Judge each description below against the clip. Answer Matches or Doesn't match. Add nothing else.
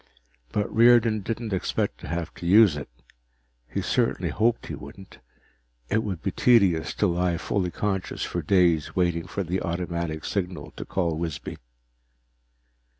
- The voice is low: Matches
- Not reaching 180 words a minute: Matches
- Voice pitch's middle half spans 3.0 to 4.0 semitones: Matches